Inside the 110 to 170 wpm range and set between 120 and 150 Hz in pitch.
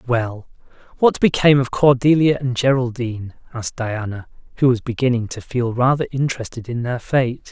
Yes: average, 150 wpm; low, 125 Hz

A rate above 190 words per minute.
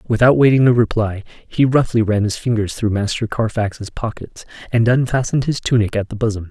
No: average, 185 wpm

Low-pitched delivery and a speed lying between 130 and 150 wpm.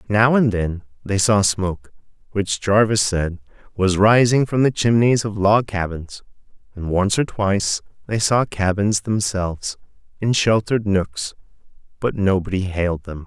Yes: low, 100 Hz; average, 145 wpm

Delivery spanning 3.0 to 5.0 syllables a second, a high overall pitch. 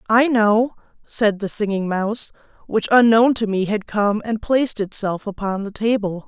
Yes: 4.7 syllables/s; high, 215 Hz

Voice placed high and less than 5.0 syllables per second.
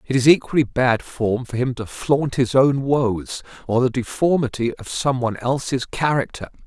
No: low, 130 Hz; 4.7 syllables/s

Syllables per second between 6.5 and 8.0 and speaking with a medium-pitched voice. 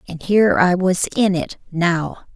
No: 4.5 syllables/s; medium, 180 Hz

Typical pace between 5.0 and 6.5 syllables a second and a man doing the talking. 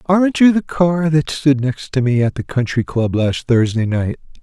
No: 4.6 syllables/s; male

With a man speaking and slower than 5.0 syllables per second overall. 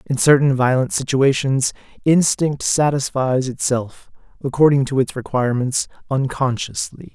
Yes: male; 4.5 syllables/s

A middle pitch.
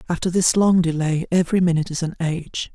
Yes: medium, 170 Hz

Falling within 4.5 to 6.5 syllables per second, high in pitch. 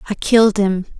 Yes: 5.8 syllables/s; high, 205 Hz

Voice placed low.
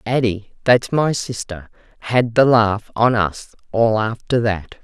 Yes: low, 110 Hz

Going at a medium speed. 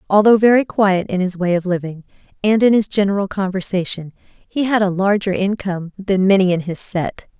Yes: average, 185 wpm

